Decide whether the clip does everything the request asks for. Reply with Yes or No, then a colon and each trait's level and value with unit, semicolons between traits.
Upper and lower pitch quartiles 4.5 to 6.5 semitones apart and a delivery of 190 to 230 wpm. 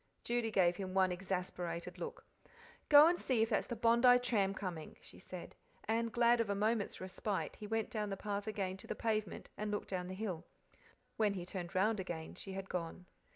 No: average, 3.3 semitones; average, 200 wpm